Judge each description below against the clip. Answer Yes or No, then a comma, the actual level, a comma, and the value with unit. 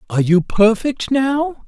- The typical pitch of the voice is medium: No, high, 235 Hz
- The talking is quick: No, average, 145 wpm